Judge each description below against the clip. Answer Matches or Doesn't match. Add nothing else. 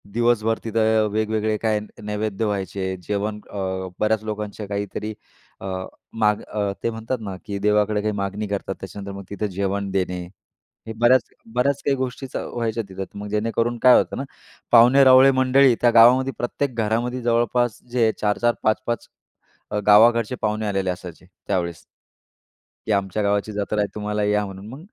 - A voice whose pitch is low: Matches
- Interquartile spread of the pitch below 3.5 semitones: Matches